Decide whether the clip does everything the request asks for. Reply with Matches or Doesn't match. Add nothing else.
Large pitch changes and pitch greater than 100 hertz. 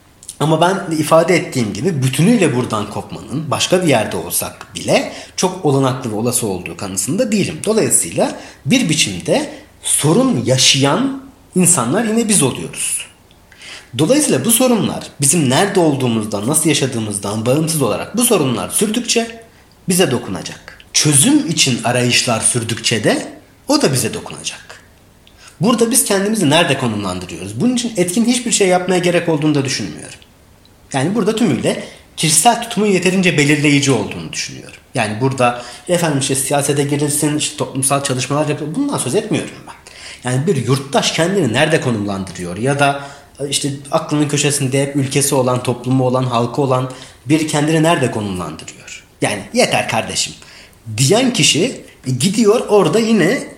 Matches